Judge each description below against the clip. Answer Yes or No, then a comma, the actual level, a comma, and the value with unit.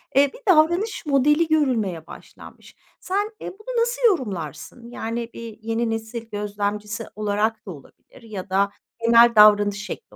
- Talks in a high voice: Yes, high, 225 Hz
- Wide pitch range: Yes, wide, 6.1 semitones